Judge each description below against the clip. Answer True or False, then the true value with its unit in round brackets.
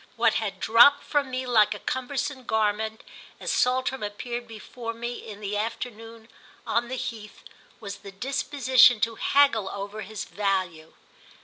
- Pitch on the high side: True (225 Hz)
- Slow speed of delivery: False (145 wpm)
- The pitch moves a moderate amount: True (3.3 semitones)